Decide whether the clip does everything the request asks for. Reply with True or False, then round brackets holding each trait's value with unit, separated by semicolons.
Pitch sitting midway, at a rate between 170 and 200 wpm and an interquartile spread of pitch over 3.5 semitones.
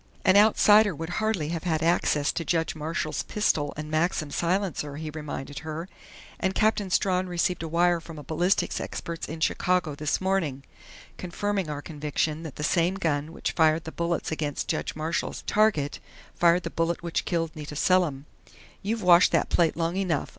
False (165 Hz; 175 wpm; 2.9 semitones)